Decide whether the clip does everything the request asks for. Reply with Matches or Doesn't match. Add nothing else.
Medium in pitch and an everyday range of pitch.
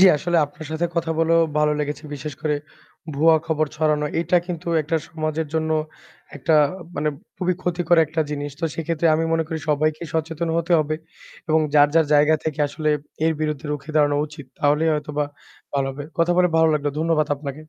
Doesn't match